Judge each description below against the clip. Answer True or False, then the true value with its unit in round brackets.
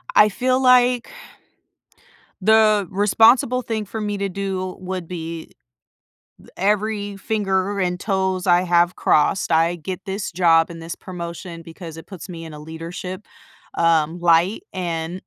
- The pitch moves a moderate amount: True (3.4 semitones)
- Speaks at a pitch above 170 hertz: True (185 Hz)